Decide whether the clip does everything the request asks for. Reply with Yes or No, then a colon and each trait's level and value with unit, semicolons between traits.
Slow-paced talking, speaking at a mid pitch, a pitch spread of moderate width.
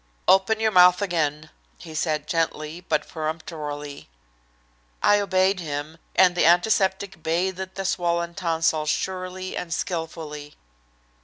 Yes: slow, 120 wpm; medium, 170 Hz; average, 3.2 semitones